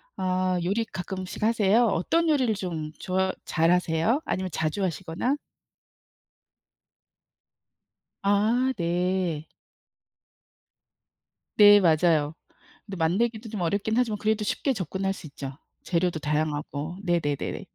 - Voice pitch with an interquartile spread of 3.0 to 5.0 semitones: Yes, average, 4.3 semitones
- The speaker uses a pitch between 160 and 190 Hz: Yes, medium, 185 Hz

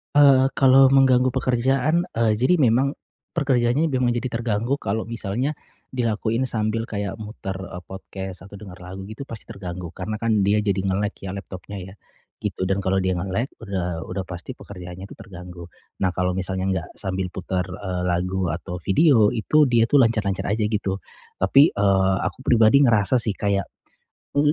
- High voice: No, low, 105 Hz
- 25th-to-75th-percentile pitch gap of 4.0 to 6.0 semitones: Yes, average, 4.3 semitones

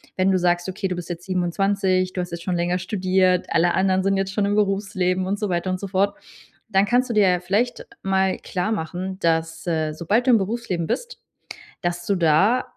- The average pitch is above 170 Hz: Yes, medium, 185 Hz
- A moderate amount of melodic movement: No, narrow, 2.2 semitones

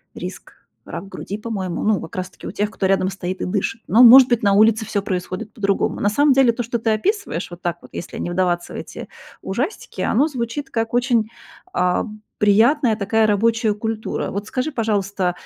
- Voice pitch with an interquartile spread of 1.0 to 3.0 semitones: No, average, 3.4 semitones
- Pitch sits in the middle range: No, high, 215 Hz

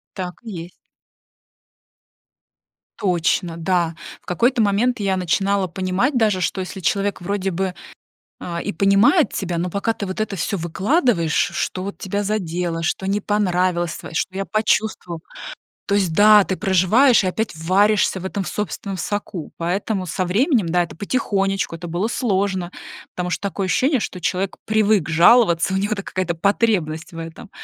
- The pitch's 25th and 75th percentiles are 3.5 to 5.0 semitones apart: No, average, 3.0 semitones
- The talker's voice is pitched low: No, high, 190 Hz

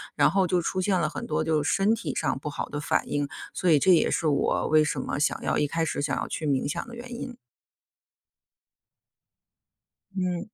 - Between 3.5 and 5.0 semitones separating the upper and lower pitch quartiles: Yes, average, 4.1 semitones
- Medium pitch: Yes, medium, 160 Hz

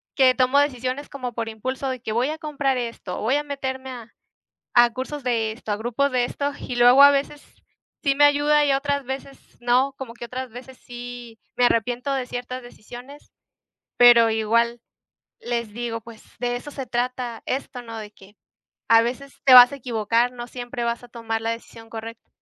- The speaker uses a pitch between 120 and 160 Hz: No, high, 245 Hz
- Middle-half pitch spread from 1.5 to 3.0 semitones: Yes, narrow, 2.5 semitones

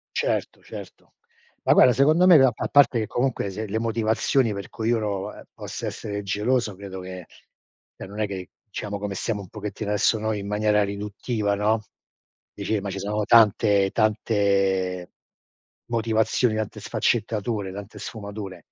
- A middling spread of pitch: No, narrow, 2.1 semitones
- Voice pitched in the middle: No, low, 105 Hz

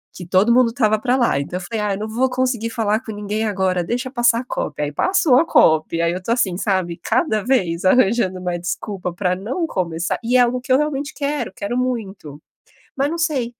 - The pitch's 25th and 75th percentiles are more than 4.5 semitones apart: Yes, wide, 5.5 semitones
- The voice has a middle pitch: No, high, 220 Hz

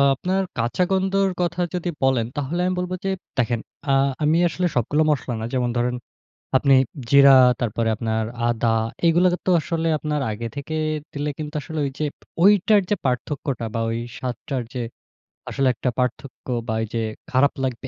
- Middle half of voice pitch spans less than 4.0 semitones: No, wide, 5.6 semitones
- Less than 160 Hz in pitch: Yes, medium, 140 Hz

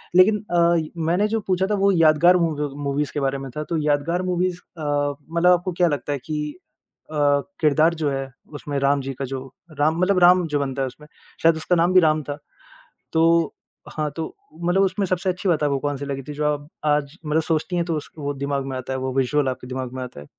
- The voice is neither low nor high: Yes, medium, 150 Hz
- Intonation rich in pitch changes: No, average, 3.4 semitones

